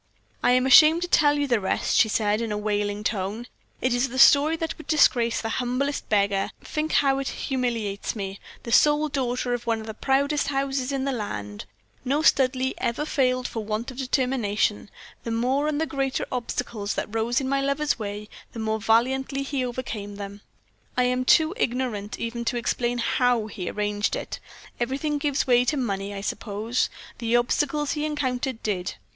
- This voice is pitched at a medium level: No, high, 245 Hz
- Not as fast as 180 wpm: No, average, 185 wpm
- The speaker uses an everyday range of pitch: Yes, average, 4.0 semitones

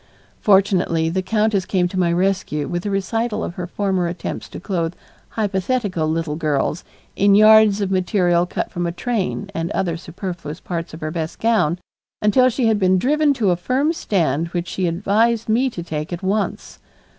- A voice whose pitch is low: No, medium, 185 Hz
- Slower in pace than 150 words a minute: No, average, 180 wpm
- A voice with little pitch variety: No, average, 3.7 semitones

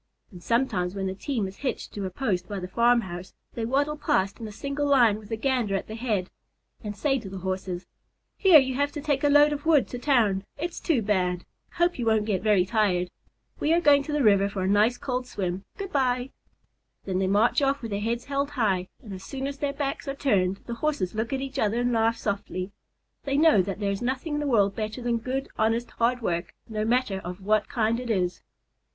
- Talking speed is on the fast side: Yes, fast, 230 wpm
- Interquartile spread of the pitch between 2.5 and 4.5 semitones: No, wide, 5.6 semitones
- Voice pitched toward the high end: Yes, high, 230 Hz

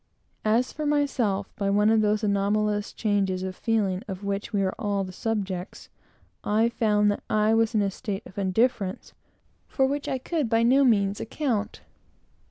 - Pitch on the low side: No, high, 210 Hz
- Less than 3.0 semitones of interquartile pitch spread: Yes, narrow, 2.4 semitones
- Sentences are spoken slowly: No, average, 175 wpm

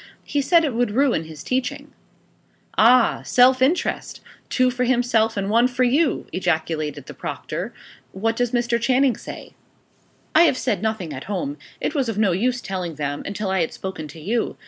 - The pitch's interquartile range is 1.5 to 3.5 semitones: No, average, 5.1 semitones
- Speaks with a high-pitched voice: Yes, high, 230 Hz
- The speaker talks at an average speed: Yes, average, 180 wpm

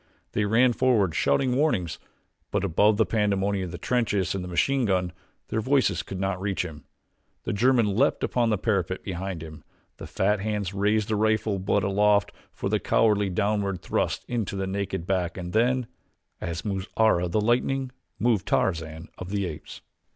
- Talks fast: No, average, 175 wpm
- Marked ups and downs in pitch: No, average, 3.1 semitones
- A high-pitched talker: No, low, 100 Hz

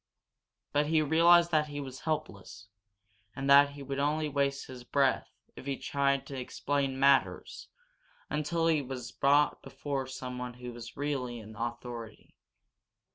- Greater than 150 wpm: No, average, 145 wpm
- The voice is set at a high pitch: No, medium, 140 Hz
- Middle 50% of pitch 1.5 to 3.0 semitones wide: Yes, narrow, 2.6 semitones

